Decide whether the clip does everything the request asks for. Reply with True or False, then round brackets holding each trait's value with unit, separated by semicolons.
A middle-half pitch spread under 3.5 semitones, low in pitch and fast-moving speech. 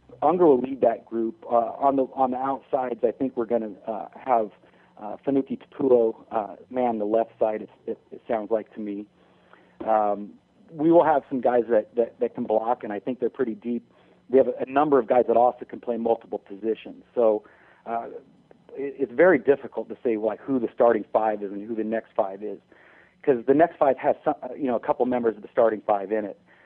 True (2.4 semitones; 115 Hz; 225 wpm)